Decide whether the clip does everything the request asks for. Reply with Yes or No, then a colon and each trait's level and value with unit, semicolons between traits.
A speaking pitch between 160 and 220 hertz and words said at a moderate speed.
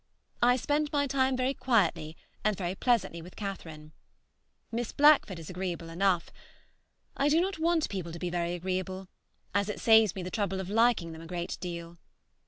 Yes: high, 190 Hz; average, 180 wpm